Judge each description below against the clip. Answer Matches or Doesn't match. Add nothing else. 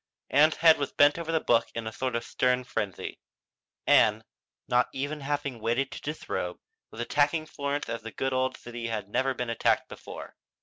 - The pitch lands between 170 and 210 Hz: Doesn't match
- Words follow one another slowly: Doesn't match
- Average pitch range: Matches